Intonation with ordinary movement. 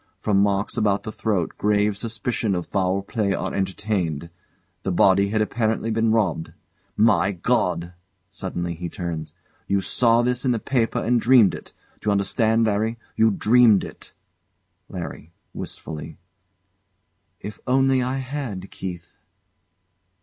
Yes: average, 3.3 semitones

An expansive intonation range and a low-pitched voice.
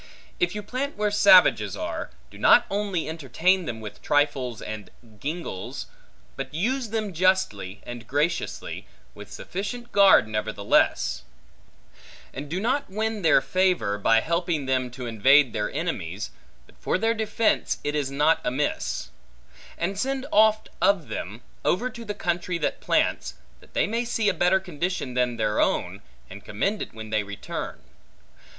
No: wide, 9.0 semitones; medium, 165 Hz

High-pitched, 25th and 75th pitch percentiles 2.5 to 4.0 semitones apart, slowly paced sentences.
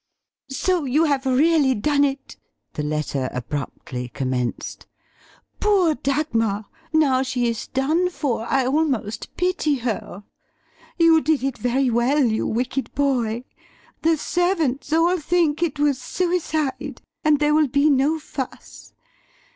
No: very high, 275 Hz; average, 4.5 semitones; slow, 130 wpm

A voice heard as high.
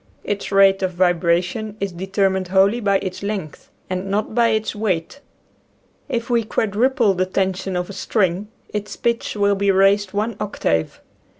Yes: high, 195 Hz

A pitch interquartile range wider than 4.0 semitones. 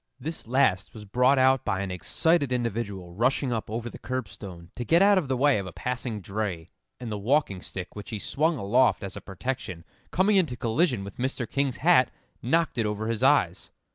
Yes: average, 5.1 semitones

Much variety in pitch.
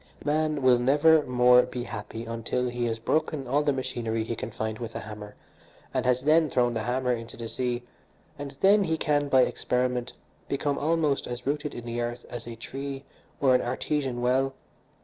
No: average, 3.1 semitones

